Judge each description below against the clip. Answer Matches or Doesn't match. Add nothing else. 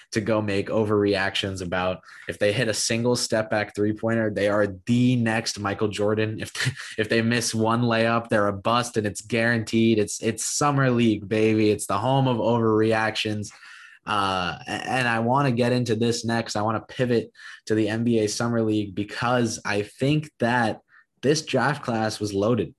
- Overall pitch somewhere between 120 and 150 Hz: Doesn't match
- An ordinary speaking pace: Matches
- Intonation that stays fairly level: Matches